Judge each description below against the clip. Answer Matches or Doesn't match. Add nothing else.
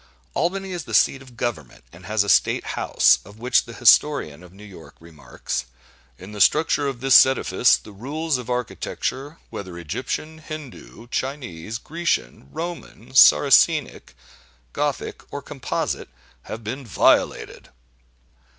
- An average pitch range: Doesn't match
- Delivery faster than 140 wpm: Doesn't match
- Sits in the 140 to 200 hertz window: Doesn't match